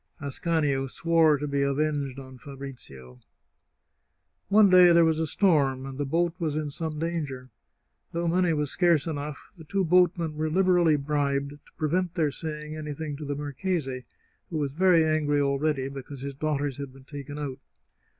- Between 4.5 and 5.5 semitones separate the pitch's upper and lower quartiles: No, average, 3.0 semitones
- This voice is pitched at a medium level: Yes, medium, 150 Hz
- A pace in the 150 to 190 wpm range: Yes, average, 170 wpm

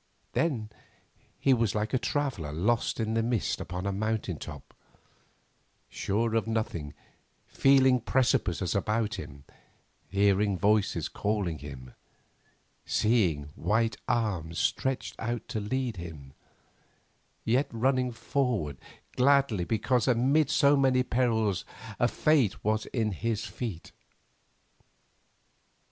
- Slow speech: Yes, slow, 110 wpm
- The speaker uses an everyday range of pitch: Yes, average, 4.5 semitones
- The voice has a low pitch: Yes, low, 110 Hz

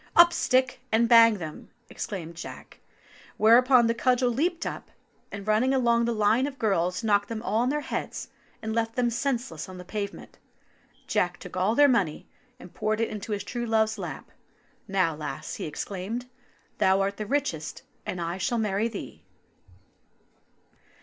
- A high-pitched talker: Yes, high, 220 Hz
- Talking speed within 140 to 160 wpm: No, average, 170 wpm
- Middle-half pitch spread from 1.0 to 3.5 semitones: No, average, 4.0 semitones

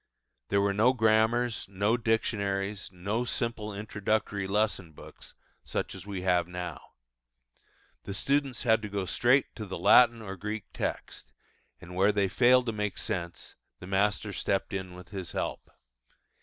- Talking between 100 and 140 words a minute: No, average, 155 wpm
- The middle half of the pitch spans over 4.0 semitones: No, average, 2.7 semitones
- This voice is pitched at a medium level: No, low, 105 Hz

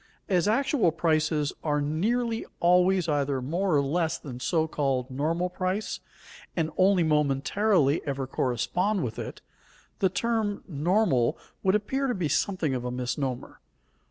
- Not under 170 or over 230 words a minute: No, average, 140 wpm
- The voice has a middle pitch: Yes, medium, 165 Hz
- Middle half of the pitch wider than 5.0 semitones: Yes, wide, 5.5 semitones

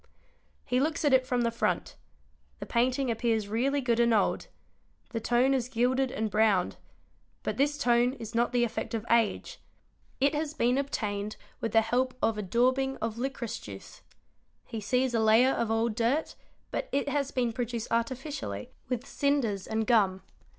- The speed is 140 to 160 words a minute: No, average, 170 wpm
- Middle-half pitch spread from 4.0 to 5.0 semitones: No, average, 2.7 semitones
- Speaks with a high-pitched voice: Yes, high, 240 Hz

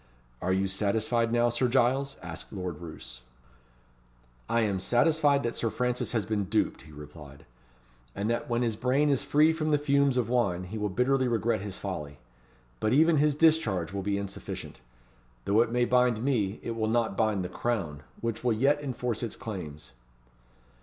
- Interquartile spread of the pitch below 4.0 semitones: No, average, 4.5 semitones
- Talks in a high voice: No, low, 115 Hz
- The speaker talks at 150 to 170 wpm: No, average, 180 wpm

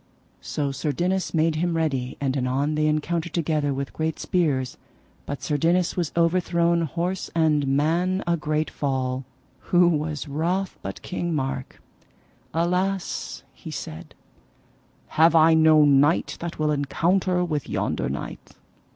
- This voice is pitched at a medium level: Yes, medium, 160 Hz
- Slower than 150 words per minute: Yes, average, 140 wpm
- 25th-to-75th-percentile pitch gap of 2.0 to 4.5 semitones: Yes, average, 3.1 semitones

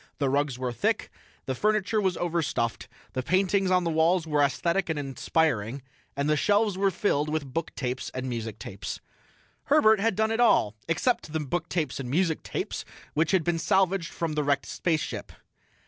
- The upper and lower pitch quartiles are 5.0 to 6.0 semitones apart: Yes, average, 5.3 semitones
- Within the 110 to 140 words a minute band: No, average, 165 wpm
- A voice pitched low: No, medium, 160 Hz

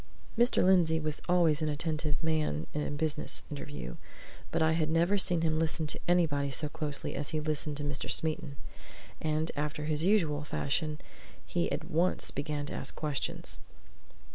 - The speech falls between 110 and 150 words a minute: No, average, 165 wpm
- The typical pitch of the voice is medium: Yes, medium, 155 Hz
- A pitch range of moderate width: No, narrow, 1.8 semitones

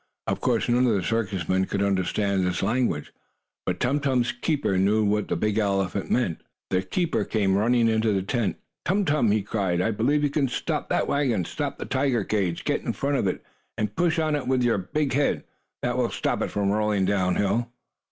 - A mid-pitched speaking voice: No, low, 110 Hz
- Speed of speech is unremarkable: No, fast, 210 wpm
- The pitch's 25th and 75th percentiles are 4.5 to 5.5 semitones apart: Yes, average, 4.8 semitones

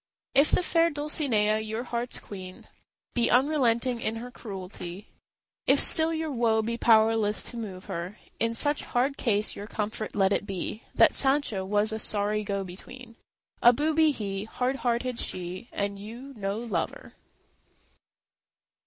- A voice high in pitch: Yes, high, 225 Hz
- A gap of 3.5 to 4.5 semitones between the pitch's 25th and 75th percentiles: Yes, average, 3.8 semitones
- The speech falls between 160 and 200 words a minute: No, average, 150 wpm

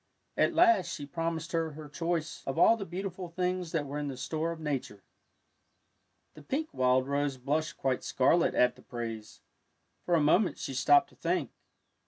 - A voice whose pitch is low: No, medium, 155 Hz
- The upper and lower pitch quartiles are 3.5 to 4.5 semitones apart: Yes, average, 4.2 semitones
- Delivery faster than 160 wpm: Yes, average, 180 wpm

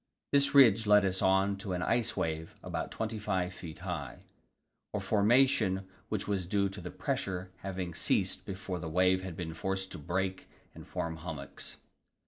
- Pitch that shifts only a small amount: Yes, narrow, 2.3 semitones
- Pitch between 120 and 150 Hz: No, very low, 95 Hz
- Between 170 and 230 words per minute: No, average, 160 wpm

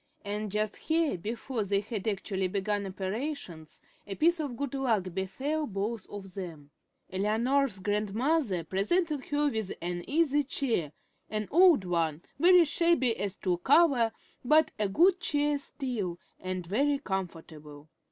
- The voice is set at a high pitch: Yes, high, 215 Hz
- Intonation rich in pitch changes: Yes, wide, 7.1 semitones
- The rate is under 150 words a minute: Yes, average, 140 wpm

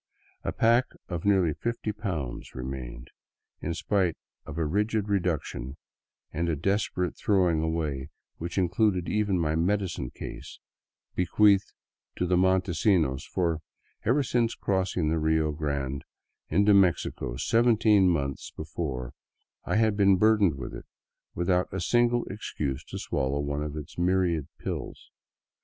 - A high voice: No, very low, 90 Hz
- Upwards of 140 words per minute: No, slow, 135 wpm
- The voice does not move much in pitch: No, average, 4.9 semitones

